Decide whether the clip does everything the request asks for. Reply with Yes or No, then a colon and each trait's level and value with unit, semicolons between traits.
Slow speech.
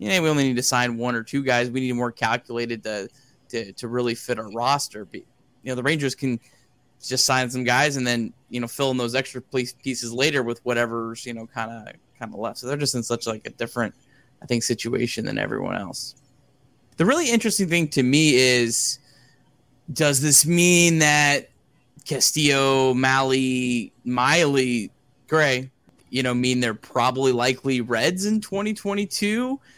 No: average, 185 wpm